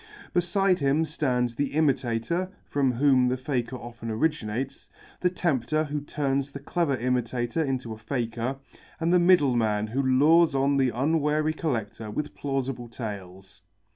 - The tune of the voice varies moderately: Yes, average, 4.2 semitones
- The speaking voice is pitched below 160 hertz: Yes, low, 135 Hz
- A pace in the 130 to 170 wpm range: Yes, average, 140 wpm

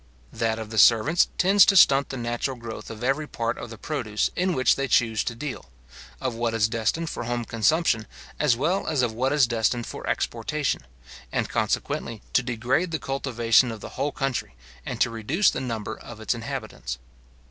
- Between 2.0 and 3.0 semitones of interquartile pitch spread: No, average, 3.4 semitones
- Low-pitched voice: Yes, low, 120 Hz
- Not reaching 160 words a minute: No, average, 190 wpm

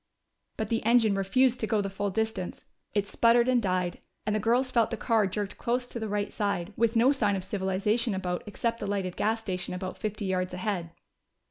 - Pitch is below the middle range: No, high, 210 Hz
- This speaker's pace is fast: Yes, fast, 210 wpm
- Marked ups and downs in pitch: No, average, 3.3 semitones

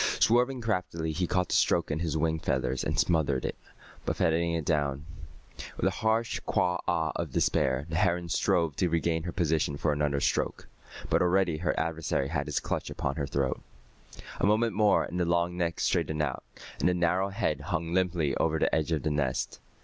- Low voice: Yes, very low, 85 Hz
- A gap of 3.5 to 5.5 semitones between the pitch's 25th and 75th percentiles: No, average, 2.8 semitones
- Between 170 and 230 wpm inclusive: Yes, average, 195 wpm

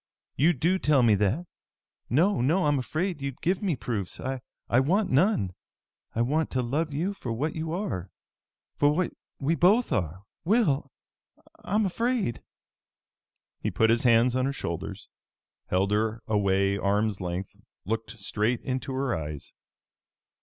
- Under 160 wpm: Yes, average, 145 wpm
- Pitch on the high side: No, low, 130 Hz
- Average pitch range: No, wide, 7.6 semitones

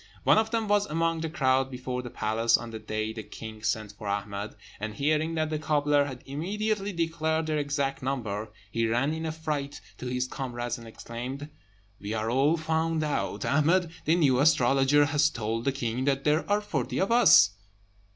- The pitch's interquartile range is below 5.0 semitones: No, average, 5.3 semitones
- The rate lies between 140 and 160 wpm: No, average, 190 wpm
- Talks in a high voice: No, medium, 140 Hz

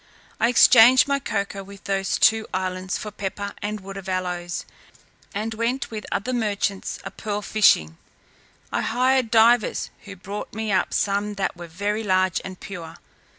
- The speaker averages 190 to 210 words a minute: No, average, 160 wpm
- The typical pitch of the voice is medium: No, high, 205 Hz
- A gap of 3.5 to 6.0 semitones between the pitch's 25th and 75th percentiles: No, average, 2.8 semitones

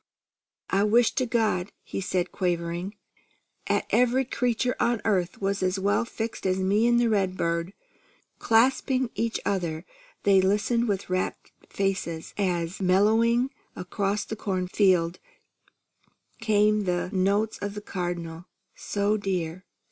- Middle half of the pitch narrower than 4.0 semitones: Yes, average, 3.4 semitones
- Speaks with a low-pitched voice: No, high, 195 Hz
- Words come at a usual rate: No, slow, 130 wpm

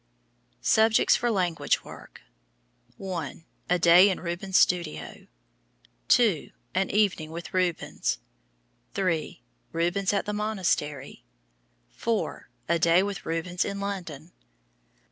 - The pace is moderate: No, slow, 105 wpm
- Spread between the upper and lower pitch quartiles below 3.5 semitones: Yes, average, 3.1 semitones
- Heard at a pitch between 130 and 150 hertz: No, medium, 180 Hz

